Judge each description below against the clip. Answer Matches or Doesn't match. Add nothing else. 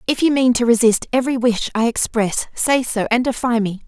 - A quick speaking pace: Matches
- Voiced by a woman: Matches